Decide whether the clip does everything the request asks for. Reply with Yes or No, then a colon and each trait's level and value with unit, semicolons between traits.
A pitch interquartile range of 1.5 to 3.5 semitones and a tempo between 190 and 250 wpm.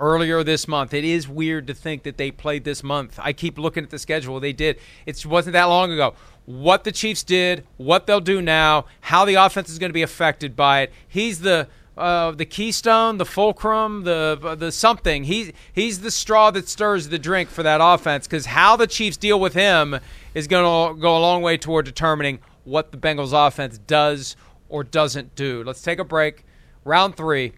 No: average, 4.0 semitones; fast, 205 wpm